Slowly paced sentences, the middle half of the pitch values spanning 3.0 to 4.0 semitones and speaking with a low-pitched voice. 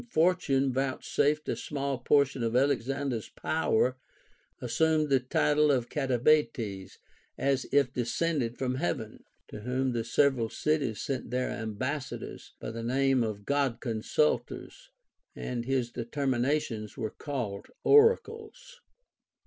Yes: slow, 120 wpm; average, 3.7 semitones; low, 130 Hz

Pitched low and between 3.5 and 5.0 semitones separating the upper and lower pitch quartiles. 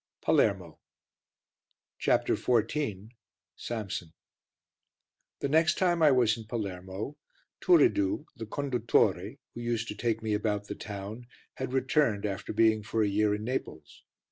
Yes: low, 110 Hz; average, 4.1 semitones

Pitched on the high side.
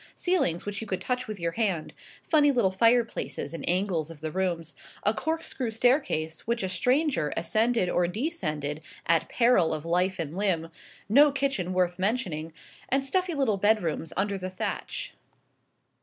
Yes: high, 195 Hz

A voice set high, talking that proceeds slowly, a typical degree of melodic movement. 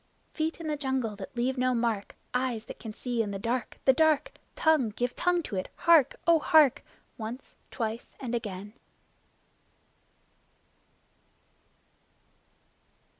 Yes: very high, 250 Hz; slow, 130 wpm; average, 4.9 semitones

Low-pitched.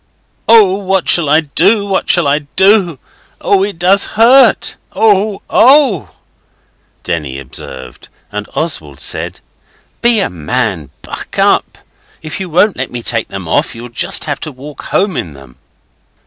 No: medium, 165 Hz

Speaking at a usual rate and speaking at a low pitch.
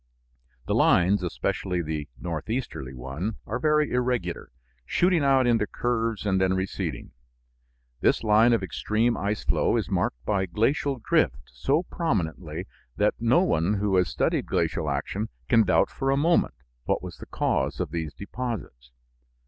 Yes: average, 150 wpm; low, 105 Hz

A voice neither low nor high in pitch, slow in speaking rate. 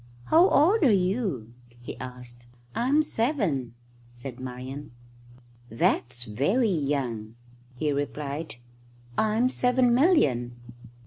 Yes: medium, 145 Hz; slow, 100 wpm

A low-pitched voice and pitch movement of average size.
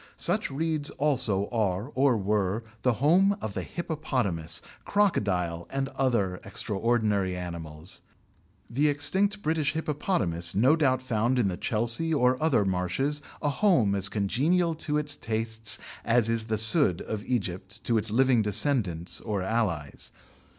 No: low, 115 Hz; wide, 6.7 semitones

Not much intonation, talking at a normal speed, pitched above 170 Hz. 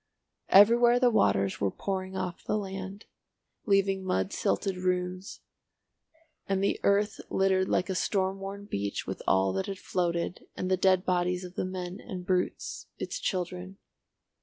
Yes: narrow, 1.5 semitones; average, 155 wpm; medium, 185 Hz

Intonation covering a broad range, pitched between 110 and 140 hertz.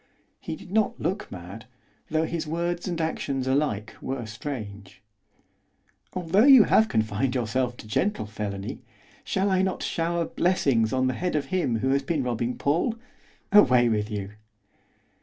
Yes: wide, 7.6 semitones; low, 135 Hz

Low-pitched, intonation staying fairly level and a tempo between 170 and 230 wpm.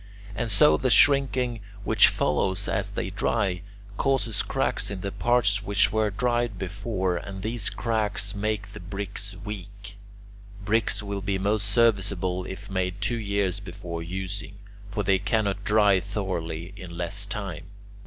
No: low, 100 Hz; narrow, 2.2 semitones; average, 145 wpm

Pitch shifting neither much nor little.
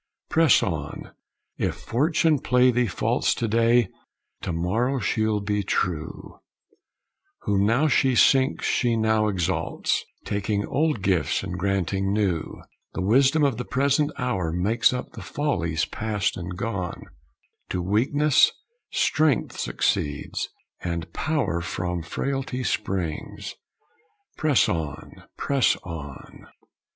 No: wide, 6.3 semitones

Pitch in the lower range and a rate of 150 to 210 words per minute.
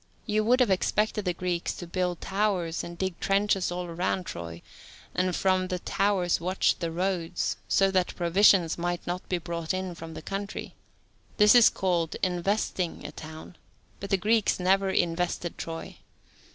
No: medium, 180 Hz; average, 165 wpm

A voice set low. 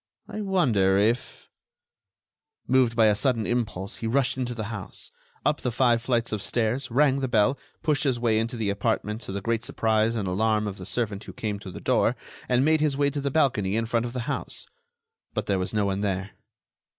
Yes: low, 115 Hz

